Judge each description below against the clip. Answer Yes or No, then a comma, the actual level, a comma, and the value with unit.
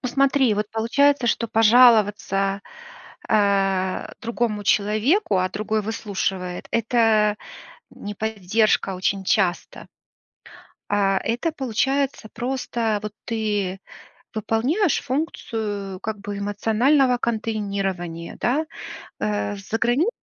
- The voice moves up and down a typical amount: Yes, average, 3.2 semitones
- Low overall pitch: No, high, 215 Hz